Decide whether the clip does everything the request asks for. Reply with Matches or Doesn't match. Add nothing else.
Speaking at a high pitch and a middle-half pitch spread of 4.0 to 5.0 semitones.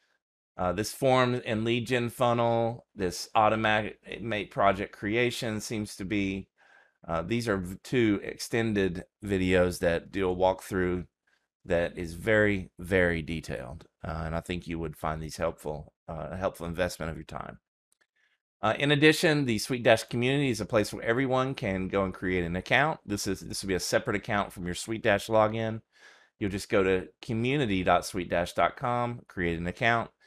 Doesn't match